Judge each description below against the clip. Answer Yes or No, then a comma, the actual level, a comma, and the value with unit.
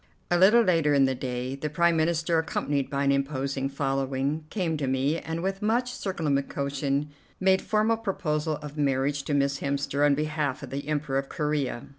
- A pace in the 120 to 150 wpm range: No, average, 180 wpm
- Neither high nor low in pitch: Yes, medium, 145 Hz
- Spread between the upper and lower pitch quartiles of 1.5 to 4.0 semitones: Yes, average, 3.0 semitones